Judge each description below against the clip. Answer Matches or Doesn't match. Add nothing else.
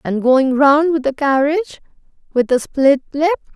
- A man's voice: Doesn't match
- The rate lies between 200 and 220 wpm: Doesn't match